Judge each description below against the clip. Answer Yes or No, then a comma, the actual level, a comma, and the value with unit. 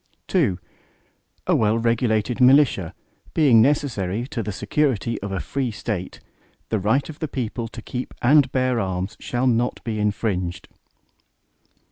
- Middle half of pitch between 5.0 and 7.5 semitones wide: No, average, 3.8 semitones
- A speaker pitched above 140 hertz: No, low, 115 Hz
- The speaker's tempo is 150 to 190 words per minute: No, average, 140 wpm